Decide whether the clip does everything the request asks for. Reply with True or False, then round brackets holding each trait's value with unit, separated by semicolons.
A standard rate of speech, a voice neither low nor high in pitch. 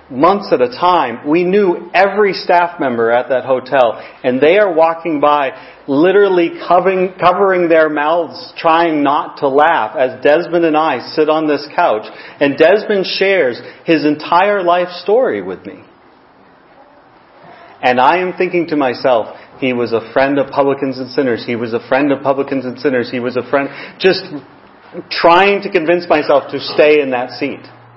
True (170 wpm; 155 Hz)